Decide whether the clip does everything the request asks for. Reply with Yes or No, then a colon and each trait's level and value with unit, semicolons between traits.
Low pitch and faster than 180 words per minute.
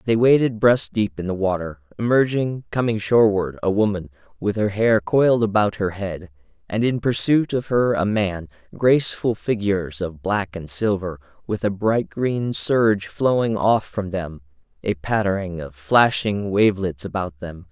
No: low, 100 Hz; average, 165 wpm